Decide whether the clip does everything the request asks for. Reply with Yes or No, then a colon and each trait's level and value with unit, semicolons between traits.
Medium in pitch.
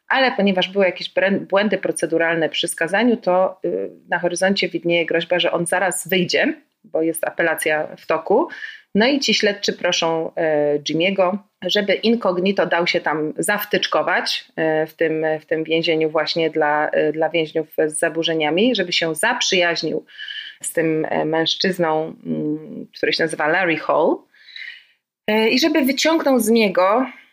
Yes: medium, 175 Hz